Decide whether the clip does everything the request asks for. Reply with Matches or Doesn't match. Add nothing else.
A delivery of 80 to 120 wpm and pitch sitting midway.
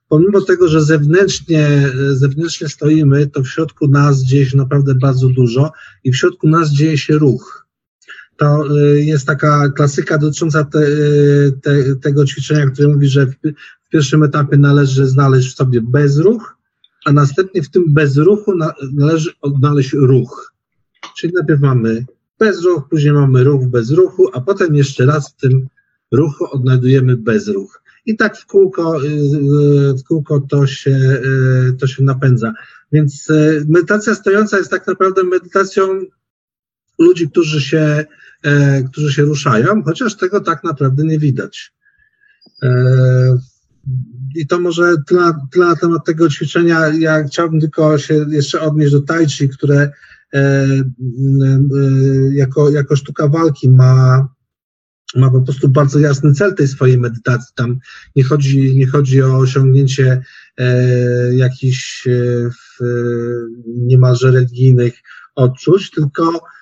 Doesn't match